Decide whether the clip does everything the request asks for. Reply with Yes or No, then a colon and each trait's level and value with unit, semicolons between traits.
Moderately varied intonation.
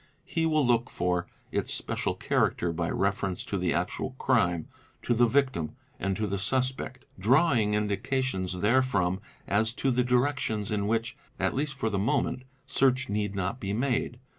Yes: average, 4.9 semitones